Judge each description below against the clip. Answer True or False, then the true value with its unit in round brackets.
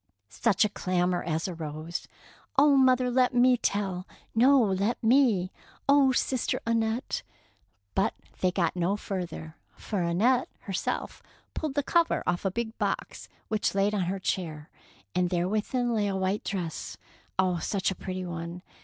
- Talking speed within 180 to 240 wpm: False (170 wpm)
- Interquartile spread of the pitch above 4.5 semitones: True (5.1 semitones)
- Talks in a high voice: True (195 Hz)